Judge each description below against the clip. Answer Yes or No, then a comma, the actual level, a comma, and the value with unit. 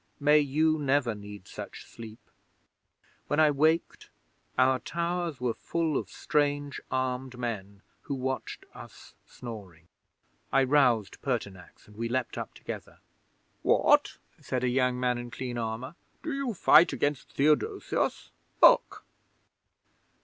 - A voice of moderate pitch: No, low, 130 Hz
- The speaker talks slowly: Yes, slow, 130 wpm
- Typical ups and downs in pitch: Yes, average, 4.1 semitones